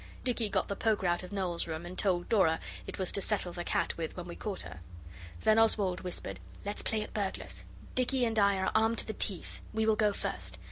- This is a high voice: Yes, high, 195 Hz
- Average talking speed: No, fast, 230 wpm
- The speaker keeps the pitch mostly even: No, average, 3.7 semitones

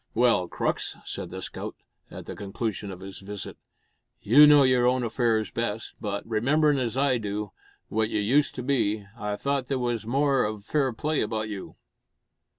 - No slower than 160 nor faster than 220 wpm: Yes, average, 175 wpm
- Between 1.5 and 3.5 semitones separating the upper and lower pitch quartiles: No, average, 4.2 semitones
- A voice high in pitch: No, low, 115 Hz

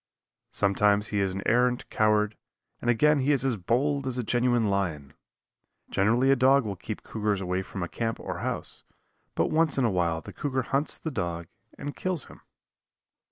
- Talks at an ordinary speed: Yes, average, 185 wpm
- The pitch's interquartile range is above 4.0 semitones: Yes, average, 5.1 semitones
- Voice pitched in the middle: No, low, 115 Hz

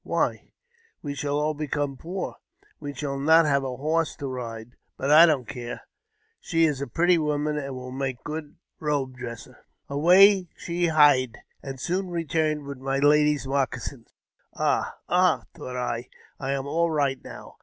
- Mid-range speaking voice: Yes, medium, 145 Hz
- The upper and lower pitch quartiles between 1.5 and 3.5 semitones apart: Yes, average, 2.8 semitones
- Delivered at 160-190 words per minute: Yes, average, 165 wpm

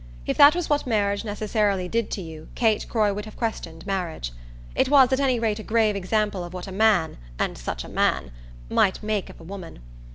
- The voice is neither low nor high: No, high, 205 Hz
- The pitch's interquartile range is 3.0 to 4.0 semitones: Yes, average, 3.7 semitones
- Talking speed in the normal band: No, fast, 215 wpm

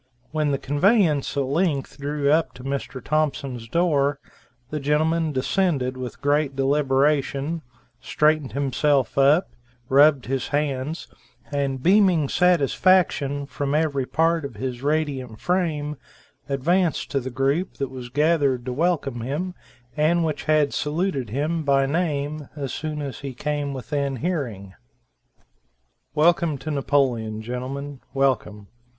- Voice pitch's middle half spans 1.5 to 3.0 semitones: Yes, narrow, 2.6 semitones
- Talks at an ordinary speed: No, slow, 130 wpm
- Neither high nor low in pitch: Yes, medium, 145 Hz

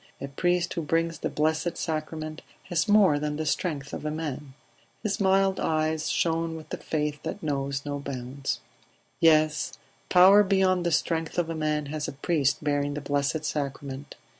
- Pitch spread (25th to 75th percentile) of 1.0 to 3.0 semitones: Yes, narrow, 2.6 semitones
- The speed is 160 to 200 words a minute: Yes, average, 170 wpm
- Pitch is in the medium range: Yes, medium, 155 Hz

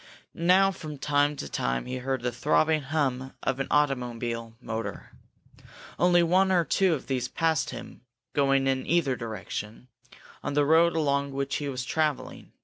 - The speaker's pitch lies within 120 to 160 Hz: Yes, medium, 140 Hz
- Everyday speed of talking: Yes, average, 160 wpm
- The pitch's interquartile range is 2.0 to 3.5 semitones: No, average, 3.9 semitones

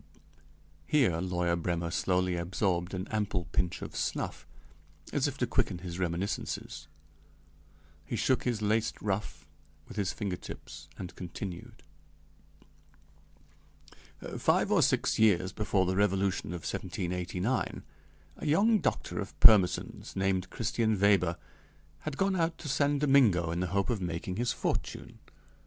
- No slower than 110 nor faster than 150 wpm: Yes, slow, 135 wpm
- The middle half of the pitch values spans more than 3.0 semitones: Yes, average, 3.8 semitones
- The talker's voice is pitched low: Yes, very low, 95 Hz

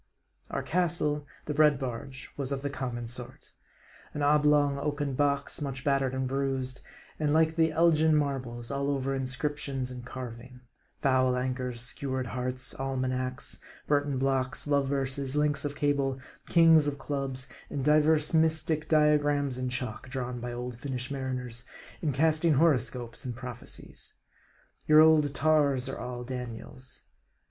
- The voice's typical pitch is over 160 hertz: No, low, 135 Hz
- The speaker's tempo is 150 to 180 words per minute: No, average, 140 wpm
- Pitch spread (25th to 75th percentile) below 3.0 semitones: Yes, narrow, 2.5 semitones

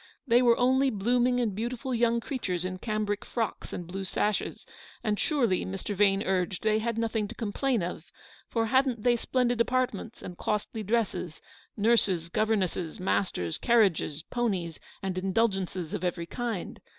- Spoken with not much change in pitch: No, average, 4.2 semitones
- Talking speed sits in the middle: Yes, average, 150 wpm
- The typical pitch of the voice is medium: No, high, 215 Hz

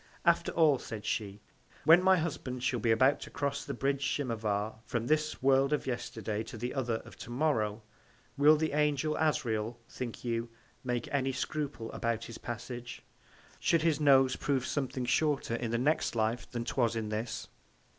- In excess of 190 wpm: No, average, 175 wpm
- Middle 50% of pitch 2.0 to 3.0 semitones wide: No, average, 3.8 semitones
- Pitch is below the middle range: Yes, low, 125 Hz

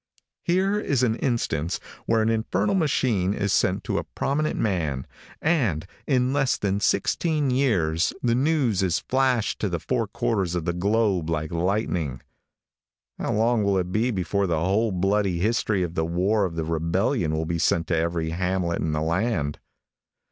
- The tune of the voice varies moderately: No, wide, 5.9 semitones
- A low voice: Yes, low, 100 Hz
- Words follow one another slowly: No, average, 170 wpm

